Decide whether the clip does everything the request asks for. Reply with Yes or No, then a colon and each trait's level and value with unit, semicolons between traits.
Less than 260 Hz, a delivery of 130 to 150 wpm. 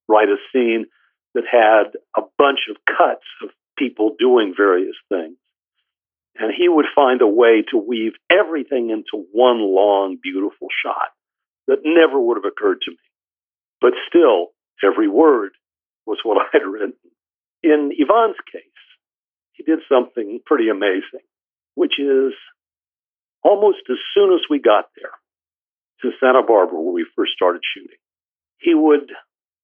No: very high, 335 Hz; average, 145 wpm